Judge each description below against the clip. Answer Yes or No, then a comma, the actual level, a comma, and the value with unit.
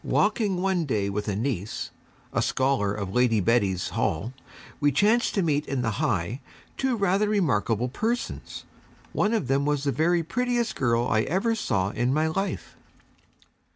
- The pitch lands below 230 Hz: Yes, medium, 140 Hz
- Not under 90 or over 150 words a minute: No, average, 160 wpm